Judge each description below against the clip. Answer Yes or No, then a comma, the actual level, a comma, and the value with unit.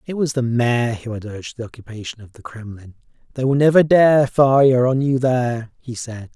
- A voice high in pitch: No, low, 125 Hz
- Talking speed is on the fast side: Yes, fast, 210 wpm